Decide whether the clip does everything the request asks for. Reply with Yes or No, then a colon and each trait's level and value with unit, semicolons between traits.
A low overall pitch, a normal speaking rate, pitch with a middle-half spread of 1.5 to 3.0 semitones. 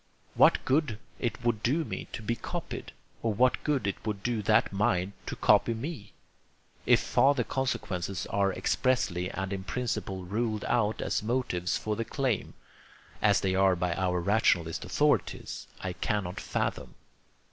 No: low, 105 Hz; average, 155 wpm; average, 4.1 semitones